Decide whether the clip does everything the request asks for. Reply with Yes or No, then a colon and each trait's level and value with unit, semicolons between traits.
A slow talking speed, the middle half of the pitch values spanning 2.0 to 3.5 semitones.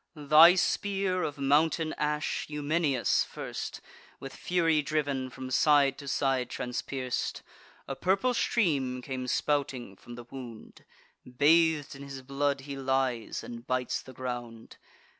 Yes: slow, 130 wpm; average, 3.1 semitones